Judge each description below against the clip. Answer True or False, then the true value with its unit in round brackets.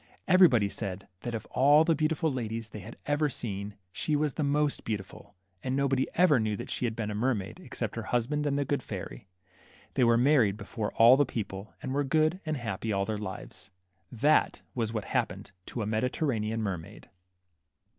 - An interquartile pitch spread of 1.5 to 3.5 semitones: False (5.2 semitones)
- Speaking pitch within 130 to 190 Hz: False (120 Hz)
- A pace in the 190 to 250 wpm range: True (195 wpm)